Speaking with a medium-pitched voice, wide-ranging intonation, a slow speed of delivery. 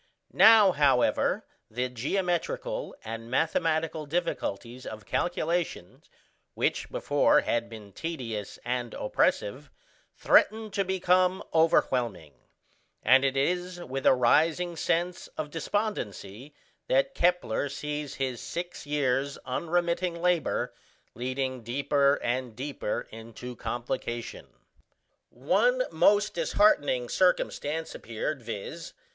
Yes: medium, 145 Hz; wide, 6.2 semitones; slow, 100 wpm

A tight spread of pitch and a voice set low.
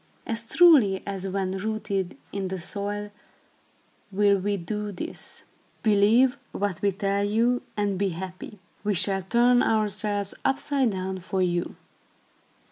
No: narrow, 2.2 semitones; high, 200 Hz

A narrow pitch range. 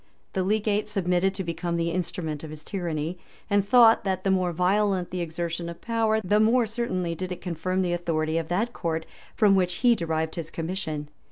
No: average, 3.3 semitones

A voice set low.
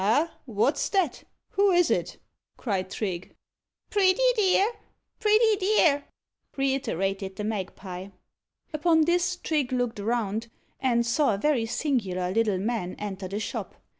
No: high, 240 Hz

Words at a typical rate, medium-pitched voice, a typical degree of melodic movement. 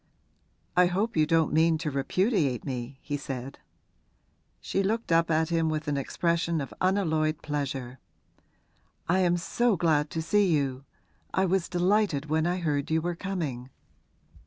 Yes: average, 155 wpm; medium, 160 Hz; average, 3.7 semitones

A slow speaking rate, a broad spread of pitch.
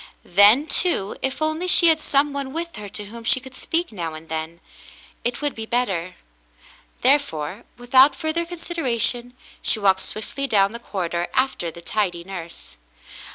No: average, 165 wpm; wide, 6.9 semitones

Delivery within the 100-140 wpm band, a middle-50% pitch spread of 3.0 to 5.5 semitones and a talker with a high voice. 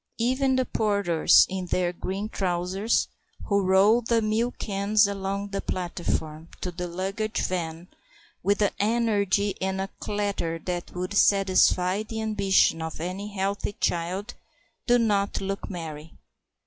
No: slow, 135 wpm; narrow, 2.6 semitones; high, 195 Hz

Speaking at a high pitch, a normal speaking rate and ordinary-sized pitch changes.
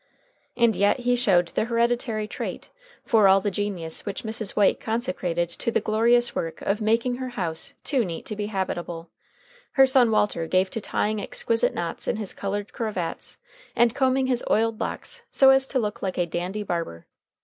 Yes: high, 215 Hz; average, 180 wpm; average, 4.2 semitones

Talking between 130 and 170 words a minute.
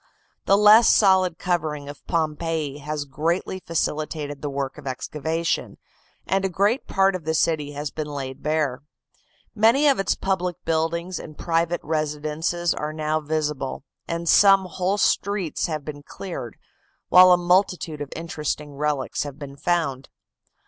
Yes: average, 150 wpm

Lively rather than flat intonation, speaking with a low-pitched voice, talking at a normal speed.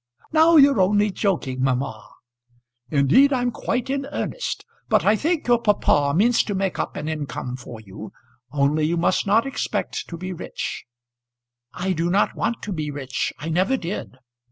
No: wide, 8.3 semitones; medium, 185 Hz; average, 170 wpm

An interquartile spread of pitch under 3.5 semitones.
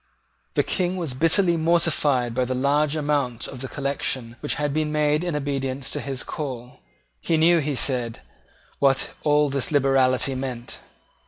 Yes: average, 2.8 semitones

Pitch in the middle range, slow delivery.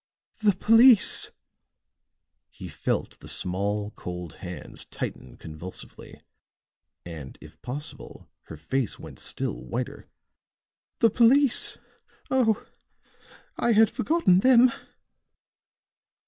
Yes: medium, 145 Hz; slow, 90 wpm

